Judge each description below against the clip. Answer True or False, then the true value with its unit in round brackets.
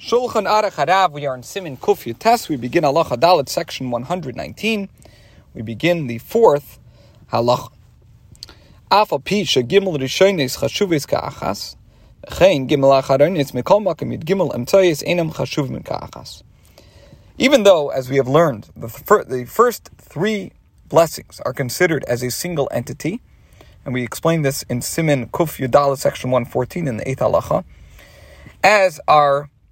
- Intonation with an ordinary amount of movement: False (6.3 semitones)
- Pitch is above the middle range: False (140 Hz)